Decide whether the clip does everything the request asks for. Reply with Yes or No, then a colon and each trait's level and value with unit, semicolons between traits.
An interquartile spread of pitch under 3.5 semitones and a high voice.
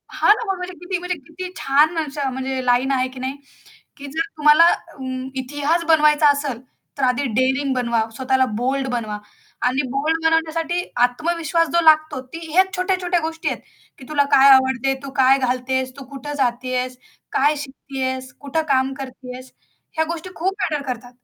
No: average, 3.8 semitones; very high, 275 Hz